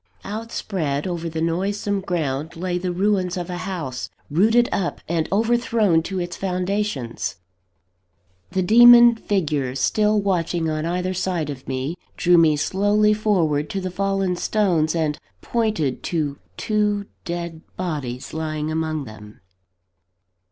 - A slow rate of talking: Yes, slow, 130 wpm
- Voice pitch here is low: No, medium, 175 Hz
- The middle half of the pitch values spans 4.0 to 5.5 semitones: Yes, average, 4.3 semitones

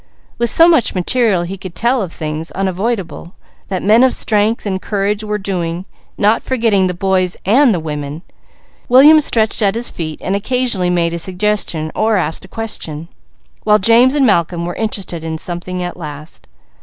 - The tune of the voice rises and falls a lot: No, average, 4.6 semitones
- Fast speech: No, average, 175 wpm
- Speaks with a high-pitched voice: Yes, high, 195 Hz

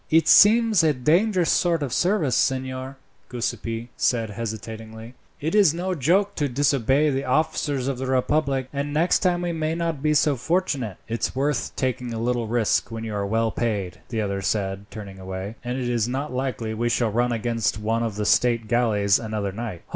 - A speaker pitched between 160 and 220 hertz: No, low, 125 Hz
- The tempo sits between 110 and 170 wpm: No, average, 190 wpm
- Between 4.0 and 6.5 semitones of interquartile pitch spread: Yes, average, 4.8 semitones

